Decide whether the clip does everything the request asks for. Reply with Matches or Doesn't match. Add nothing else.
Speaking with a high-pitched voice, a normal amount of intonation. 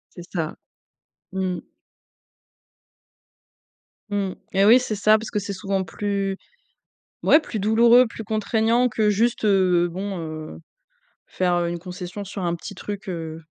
Matches